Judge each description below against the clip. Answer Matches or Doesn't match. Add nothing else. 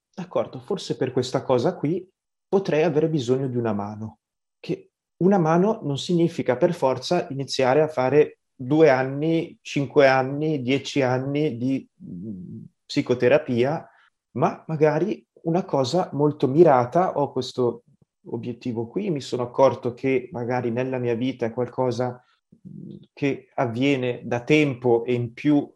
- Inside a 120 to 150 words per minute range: Matches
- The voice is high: Doesn't match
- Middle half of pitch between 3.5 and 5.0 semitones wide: Matches